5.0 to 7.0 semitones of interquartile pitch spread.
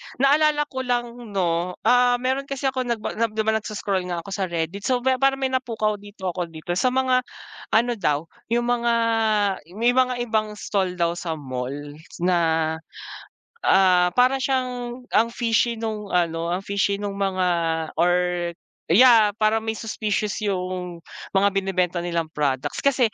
Yes: wide, 5.5 semitones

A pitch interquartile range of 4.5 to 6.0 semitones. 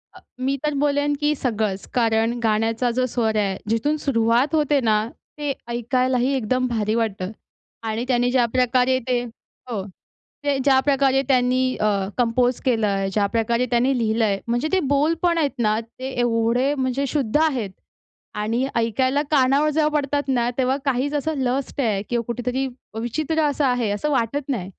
No: average, 3.3 semitones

